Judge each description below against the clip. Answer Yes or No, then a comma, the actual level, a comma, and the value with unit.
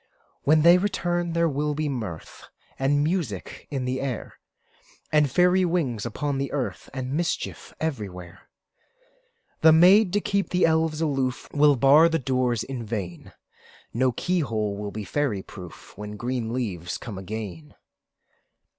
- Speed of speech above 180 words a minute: No, average, 145 wpm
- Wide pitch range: Yes, wide, 6.6 semitones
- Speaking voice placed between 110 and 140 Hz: Yes, low, 135 Hz